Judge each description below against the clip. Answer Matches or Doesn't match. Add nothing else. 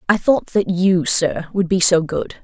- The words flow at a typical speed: Doesn't match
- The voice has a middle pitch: Matches